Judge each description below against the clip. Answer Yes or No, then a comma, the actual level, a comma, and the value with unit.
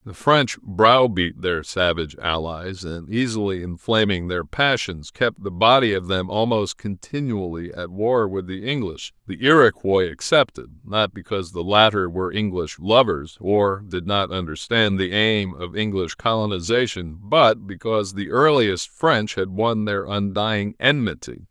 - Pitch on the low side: Yes, low, 100 Hz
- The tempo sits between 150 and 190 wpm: No, average, 140 wpm